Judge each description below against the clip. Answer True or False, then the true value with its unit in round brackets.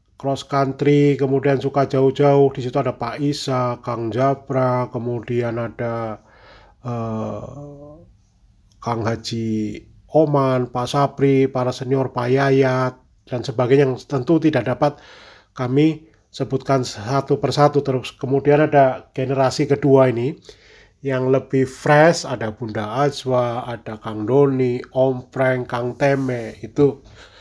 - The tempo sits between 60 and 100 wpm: False (120 wpm)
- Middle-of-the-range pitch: False (130 Hz)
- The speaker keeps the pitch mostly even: True (2.3 semitones)